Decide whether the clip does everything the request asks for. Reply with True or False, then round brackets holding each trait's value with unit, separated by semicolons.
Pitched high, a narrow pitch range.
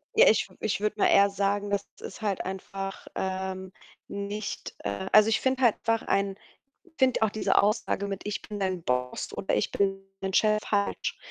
True (200 Hz; 1.7 semitones)